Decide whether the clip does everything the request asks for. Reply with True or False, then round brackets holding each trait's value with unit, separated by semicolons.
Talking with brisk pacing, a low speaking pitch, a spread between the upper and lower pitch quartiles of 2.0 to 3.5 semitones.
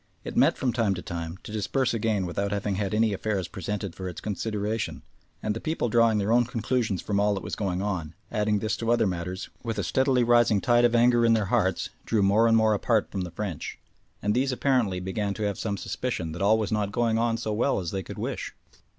True (235 wpm; 105 Hz; 3.0 semitones)